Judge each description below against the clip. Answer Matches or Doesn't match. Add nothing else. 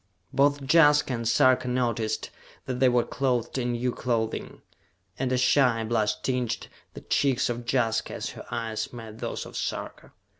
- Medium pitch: Doesn't match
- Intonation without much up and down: Matches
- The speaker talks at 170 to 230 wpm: Doesn't match